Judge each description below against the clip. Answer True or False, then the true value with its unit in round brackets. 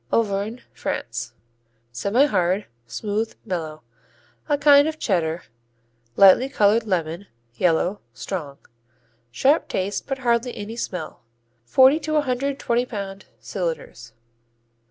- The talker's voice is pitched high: True (205 Hz)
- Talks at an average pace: False (110 wpm)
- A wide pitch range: True (6.6 semitones)